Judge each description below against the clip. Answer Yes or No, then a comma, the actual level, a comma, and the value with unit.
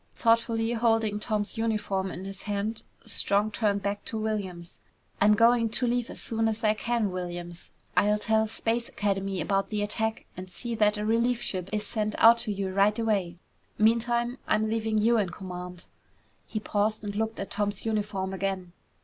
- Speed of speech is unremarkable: Yes, average, 175 wpm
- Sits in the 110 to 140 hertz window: No, high, 210 Hz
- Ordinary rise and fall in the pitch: No, narrow, 2.3 semitones